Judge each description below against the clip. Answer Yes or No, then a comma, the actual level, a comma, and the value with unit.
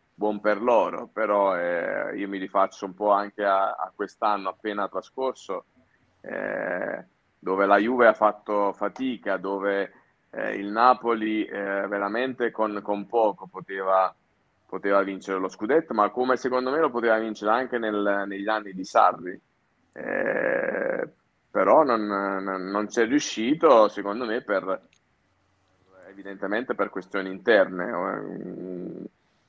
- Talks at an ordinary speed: Yes, average, 130 wpm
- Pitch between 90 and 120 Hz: Yes, low, 100 Hz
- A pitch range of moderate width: No, narrow, 2.0 semitones